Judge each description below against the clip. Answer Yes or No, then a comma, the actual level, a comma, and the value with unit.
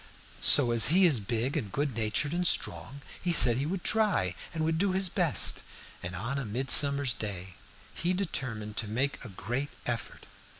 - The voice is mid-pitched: No, low, 130 Hz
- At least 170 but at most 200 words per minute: Yes, average, 175 wpm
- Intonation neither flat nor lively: No, wide, 6.5 semitones